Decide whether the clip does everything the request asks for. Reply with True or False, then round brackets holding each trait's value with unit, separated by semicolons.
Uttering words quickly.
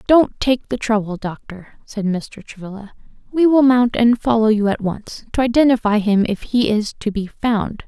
False (190 wpm)